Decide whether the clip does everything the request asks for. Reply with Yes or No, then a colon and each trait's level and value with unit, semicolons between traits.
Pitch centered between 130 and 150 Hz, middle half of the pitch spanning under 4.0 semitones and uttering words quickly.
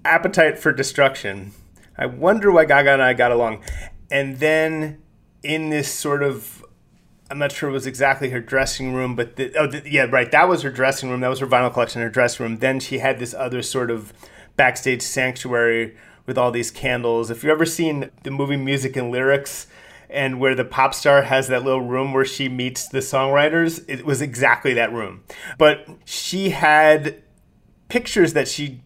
No: low, 135 Hz; average, 2.9 semitones; average, 190 wpm